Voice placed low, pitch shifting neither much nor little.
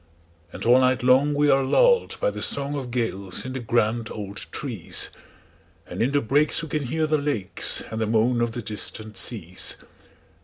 Yes: low, 125 Hz; average, 4.4 semitones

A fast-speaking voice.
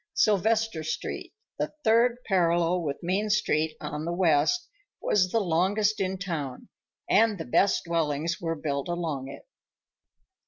No: slow, 135 wpm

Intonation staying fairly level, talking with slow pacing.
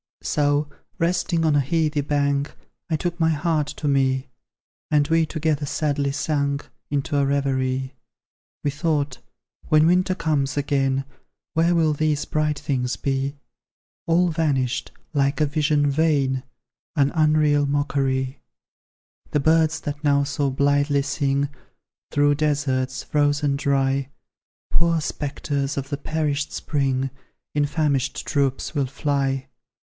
Yes: narrow, 1.9 semitones; slow, 125 wpm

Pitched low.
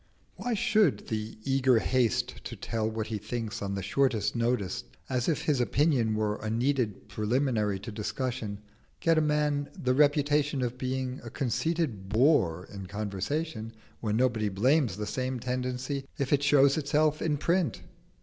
Yes: low, 125 Hz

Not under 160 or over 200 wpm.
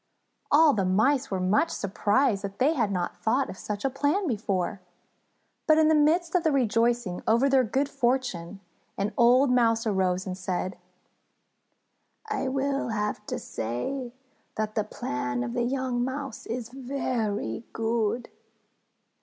No: average, 145 wpm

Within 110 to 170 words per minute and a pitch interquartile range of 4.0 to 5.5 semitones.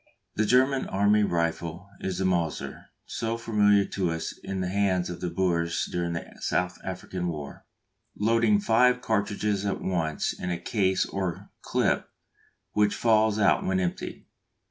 No: average, 150 wpm; average, 3.1 semitones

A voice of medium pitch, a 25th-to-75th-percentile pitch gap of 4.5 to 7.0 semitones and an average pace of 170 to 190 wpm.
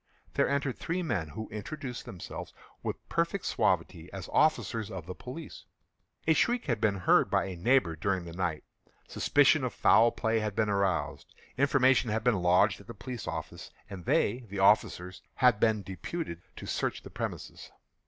No: low, 110 Hz; average, 5.3 semitones; average, 175 wpm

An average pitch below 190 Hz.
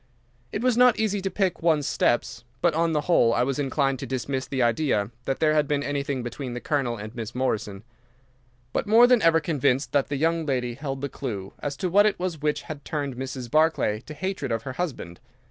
Yes: medium, 140 Hz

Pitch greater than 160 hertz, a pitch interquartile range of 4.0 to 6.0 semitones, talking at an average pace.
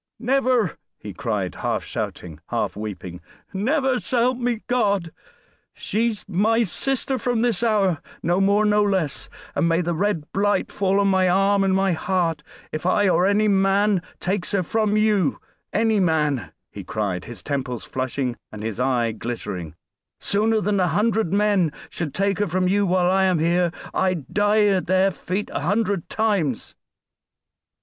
Yes: high, 190 Hz; average, 4.6 semitones; average, 160 wpm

